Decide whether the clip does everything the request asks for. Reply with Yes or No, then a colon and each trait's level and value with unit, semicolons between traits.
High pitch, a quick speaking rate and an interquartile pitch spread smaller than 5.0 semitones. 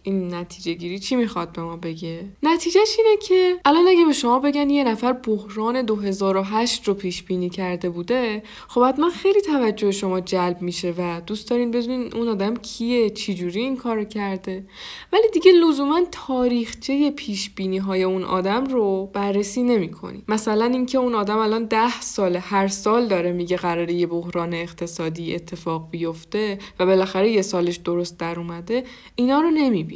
No: high, 210 Hz; fast, 170 wpm; wide, 5.6 semitones